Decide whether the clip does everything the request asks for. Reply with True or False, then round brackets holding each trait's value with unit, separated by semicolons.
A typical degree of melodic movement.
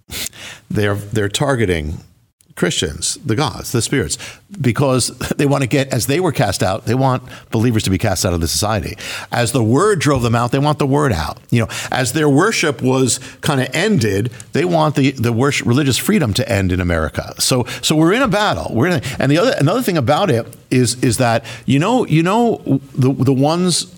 True (4.2 semitones)